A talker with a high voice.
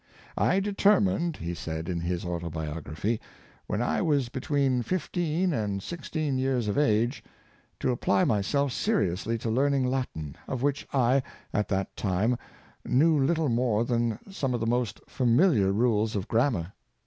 No: low, 120 Hz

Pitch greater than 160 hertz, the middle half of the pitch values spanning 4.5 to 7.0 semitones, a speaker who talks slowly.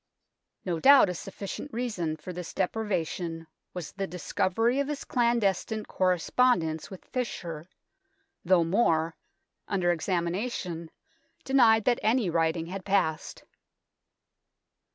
Yes: medium, 185 Hz; average, 5.1 semitones; slow, 110 wpm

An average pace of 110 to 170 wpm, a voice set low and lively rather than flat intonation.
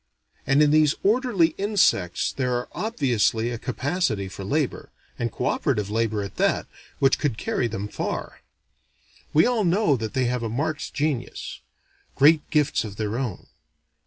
Yes: average, 160 wpm; low, 130 Hz; wide, 5.7 semitones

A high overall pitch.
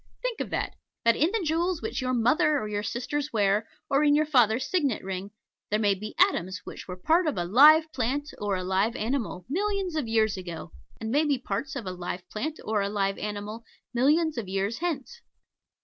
Yes: high, 235 Hz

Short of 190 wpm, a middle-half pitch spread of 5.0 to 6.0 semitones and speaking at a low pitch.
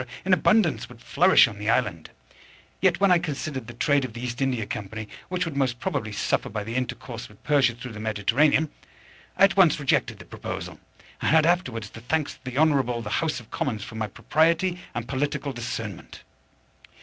No: average, 195 wpm; wide, 5.6 semitones; low, 130 Hz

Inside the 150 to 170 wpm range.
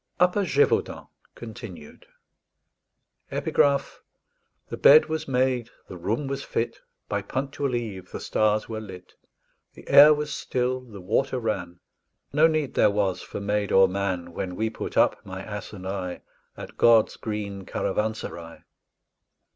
No: average, 140 wpm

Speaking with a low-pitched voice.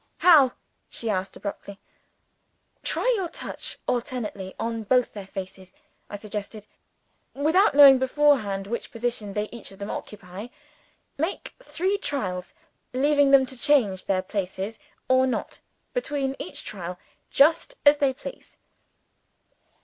No: high, 240 Hz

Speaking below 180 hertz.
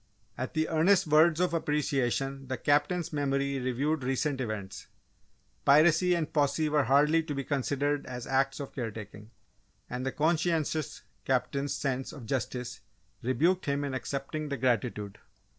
Yes: medium, 140 Hz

